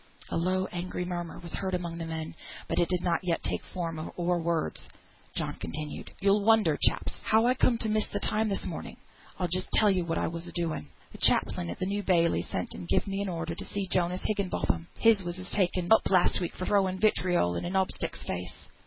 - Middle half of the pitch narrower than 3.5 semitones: Yes, average, 2.8 semitones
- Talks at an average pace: No, fast, 230 wpm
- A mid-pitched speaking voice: Yes, medium, 180 Hz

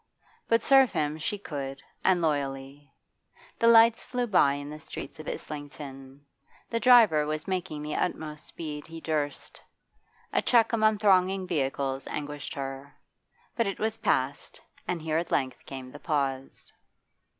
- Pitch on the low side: No, medium, 155 Hz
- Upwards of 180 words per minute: No, average, 150 wpm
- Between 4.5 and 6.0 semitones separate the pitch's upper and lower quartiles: Yes, wide, 5.5 semitones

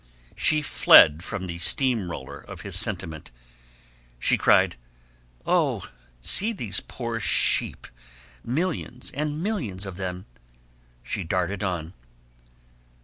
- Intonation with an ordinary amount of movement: No, wide, 7.0 semitones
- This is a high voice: No, low, 100 Hz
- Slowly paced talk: Yes, slow, 110 wpm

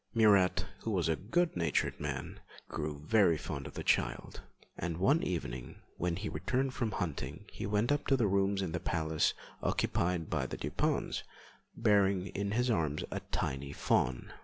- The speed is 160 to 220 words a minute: Yes, average, 170 wpm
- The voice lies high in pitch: No, very low, 90 Hz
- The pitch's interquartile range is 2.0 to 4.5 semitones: No, average, 5.3 semitones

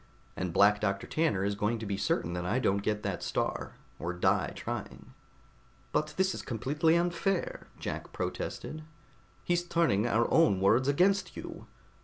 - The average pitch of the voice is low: Yes, low, 120 Hz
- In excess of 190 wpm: No, average, 160 wpm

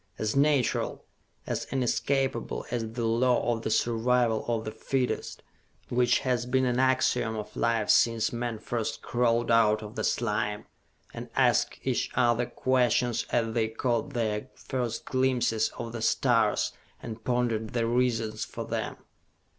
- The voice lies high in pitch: No, low, 120 Hz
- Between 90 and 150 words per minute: Yes, average, 145 wpm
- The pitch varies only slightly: Yes, narrow, 1.9 semitones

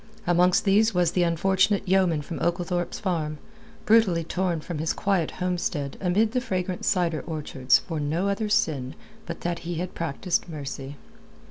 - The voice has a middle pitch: Yes, medium, 175 Hz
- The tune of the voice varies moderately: Yes, average, 3.0 semitones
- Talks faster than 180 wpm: No, average, 155 wpm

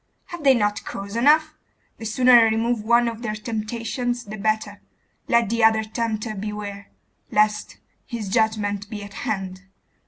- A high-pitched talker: Yes, high, 220 Hz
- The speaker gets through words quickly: No, average, 155 wpm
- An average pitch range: No, narrow, 2.2 semitones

